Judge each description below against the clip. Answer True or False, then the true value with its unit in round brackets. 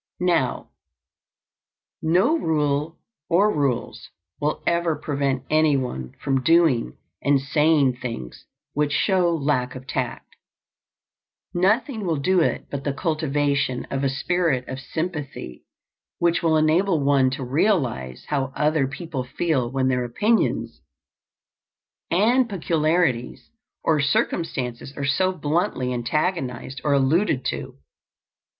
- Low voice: False (145 Hz)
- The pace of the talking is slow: True (115 wpm)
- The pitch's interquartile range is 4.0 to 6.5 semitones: True (4.3 semitones)